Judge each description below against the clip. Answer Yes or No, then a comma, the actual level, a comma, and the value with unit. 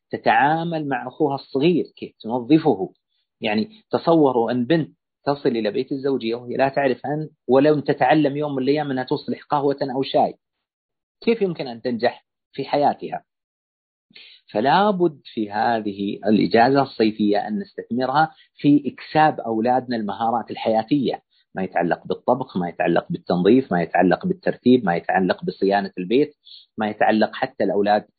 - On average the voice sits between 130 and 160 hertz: Yes, low, 135 Hz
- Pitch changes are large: No, average, 4.6 semitones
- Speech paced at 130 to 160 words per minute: Yes, fast, 135 wpm